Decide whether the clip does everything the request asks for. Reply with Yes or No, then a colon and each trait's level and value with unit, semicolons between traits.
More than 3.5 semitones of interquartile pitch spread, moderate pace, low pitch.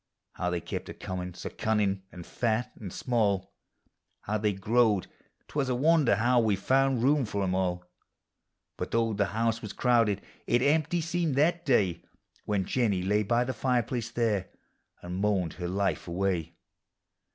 Yes: average, 4.3 semitones; average, 170 wpm; low, 110 Hz